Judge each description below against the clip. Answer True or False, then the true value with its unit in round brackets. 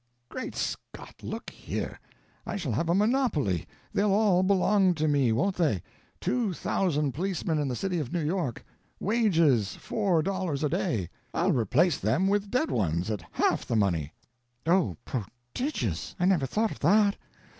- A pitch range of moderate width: False (8.0 semitones)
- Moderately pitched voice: True (170 Hz)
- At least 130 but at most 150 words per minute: False (160 wpm)